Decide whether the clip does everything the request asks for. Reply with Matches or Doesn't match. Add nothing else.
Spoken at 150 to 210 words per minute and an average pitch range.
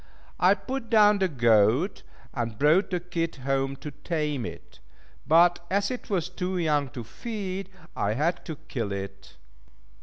Doesn't match